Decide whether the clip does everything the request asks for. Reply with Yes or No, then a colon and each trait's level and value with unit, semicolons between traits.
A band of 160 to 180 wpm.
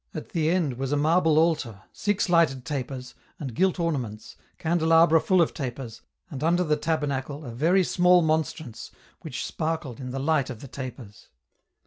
Yes: average, 175 wpm